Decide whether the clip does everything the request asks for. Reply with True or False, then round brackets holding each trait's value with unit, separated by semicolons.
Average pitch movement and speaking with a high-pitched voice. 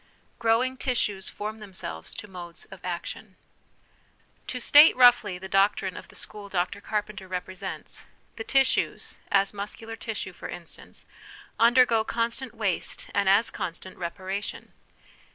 True (3.4 semitones; 205 Hz)